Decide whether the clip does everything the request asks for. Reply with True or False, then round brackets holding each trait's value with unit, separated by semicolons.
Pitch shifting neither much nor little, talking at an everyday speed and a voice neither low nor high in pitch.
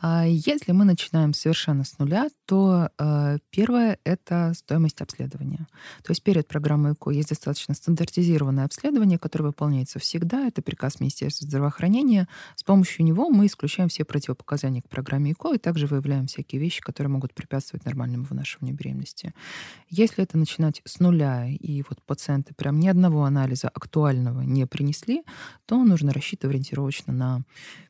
True (4.0 semitones; 150 wpm; 150 Hz)